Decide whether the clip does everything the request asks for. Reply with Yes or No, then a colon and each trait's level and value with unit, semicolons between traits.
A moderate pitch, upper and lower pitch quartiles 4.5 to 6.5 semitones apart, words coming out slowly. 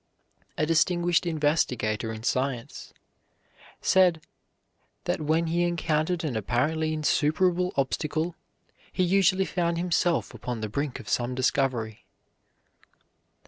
Yes: medium, 155 Hz; average, 5.1 semitones; slow, 105 wpm